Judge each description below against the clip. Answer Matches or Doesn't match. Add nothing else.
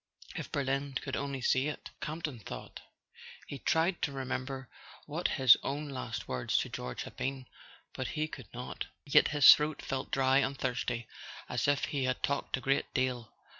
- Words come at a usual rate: Matches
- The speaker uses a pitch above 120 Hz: Matches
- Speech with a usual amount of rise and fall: Doesn't match